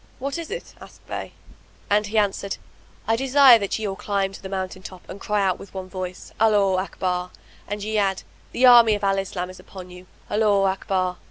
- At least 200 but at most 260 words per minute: Yes, fast, 205 wpm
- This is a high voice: Yes, high, 195 Hz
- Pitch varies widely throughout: No, narrow, 2.4 semitones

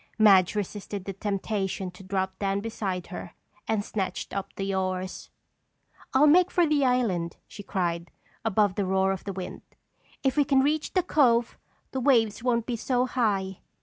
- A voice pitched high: Yes, high, 205 Hz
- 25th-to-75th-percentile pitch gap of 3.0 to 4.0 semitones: No, average, 4.6 semitones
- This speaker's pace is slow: No, average, 170 wpm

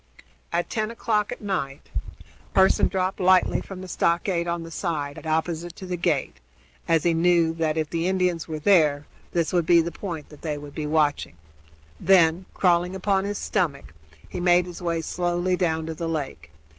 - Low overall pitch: No, medium, 170 Hz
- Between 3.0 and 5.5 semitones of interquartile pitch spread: No, narrow, 2.4 semitones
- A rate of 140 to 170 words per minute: No, average, 180 wpm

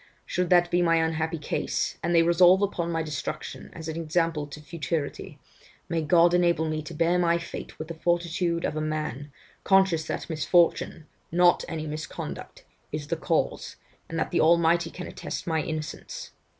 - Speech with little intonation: Yes, narrow, 1.7 semitones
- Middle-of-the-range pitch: Yes, medium, 165 Hz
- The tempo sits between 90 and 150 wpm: No, average, 175 wpm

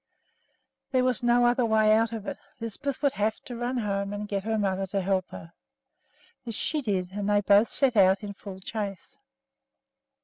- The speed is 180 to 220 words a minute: Yes, average, 190 wpm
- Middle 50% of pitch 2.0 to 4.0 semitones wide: Yes, average, 3.3 semitones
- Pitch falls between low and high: No, high, 210 Hz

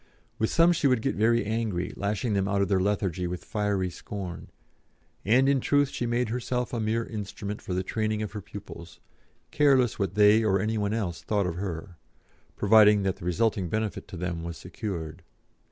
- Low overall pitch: Yes, low, 105 Hz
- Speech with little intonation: No, average, 3.3 semitones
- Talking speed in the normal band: Yes, average, 190 wpm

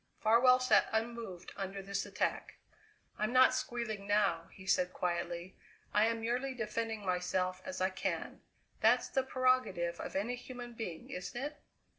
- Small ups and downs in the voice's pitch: No, average, 4.7 semitones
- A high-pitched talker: Yes, high, 215 Hz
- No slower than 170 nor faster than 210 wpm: No, average, 150 wpm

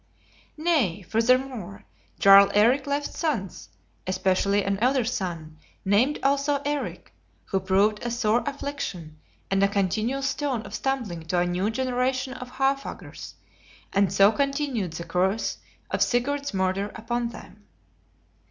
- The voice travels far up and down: Yes, wide, 5.8 semitones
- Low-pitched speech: No, high, 225 Hz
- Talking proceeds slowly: Yes, slow, 130 wpm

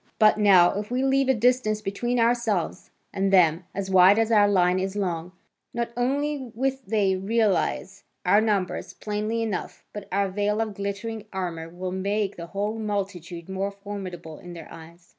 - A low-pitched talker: No, high, 200 Hz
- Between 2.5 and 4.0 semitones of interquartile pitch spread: Yes, average, 3.0 semitones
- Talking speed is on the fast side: No, average, 170 wpm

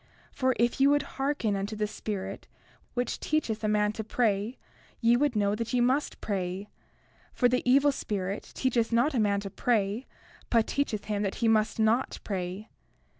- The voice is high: Yes, high, 220 Hz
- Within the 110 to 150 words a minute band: No, average, 175 wpm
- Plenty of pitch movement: No, average, 3.5 semitones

